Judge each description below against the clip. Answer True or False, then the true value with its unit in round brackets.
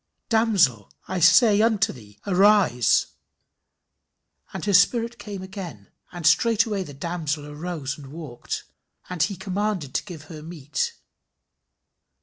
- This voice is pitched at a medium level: True (180 Hz)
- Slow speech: True (125 wpm)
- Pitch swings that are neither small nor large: False (5.7 semitones)